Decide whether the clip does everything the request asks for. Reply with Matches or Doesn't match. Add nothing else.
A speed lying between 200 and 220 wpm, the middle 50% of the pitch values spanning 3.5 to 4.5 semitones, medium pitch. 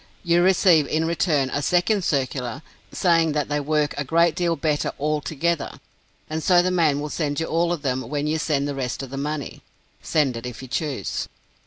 Doesn't match